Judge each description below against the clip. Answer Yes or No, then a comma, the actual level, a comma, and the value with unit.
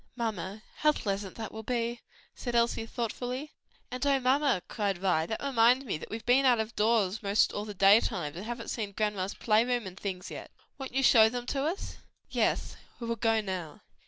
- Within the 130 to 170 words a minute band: No, fast, 205 wpm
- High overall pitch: Yes, high, 225 Hz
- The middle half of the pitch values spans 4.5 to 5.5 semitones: No, average, 3.6 semitones